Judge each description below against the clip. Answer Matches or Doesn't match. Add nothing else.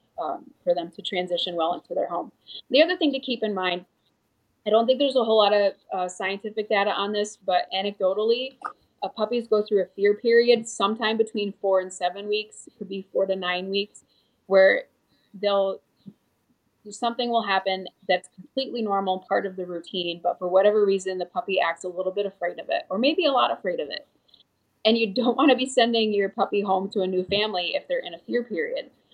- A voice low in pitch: Doesn't match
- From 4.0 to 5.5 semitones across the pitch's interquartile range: Doesn't match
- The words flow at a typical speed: Doesn't match